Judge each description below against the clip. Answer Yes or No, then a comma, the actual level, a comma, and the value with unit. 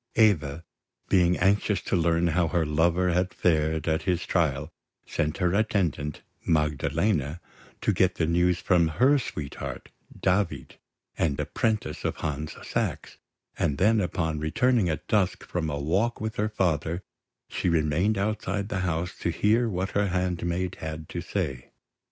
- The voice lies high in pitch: No, very low, 85 Hz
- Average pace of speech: Yes, average, 150 wpm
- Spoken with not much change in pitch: No, average, 3.7 semitones